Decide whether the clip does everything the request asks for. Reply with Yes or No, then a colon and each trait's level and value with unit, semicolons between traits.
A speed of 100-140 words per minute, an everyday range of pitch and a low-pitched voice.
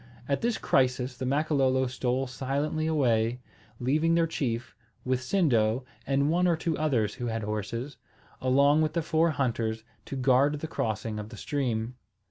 No: average, 160 wpm; average, 4.3 semitones; low, 130 Hz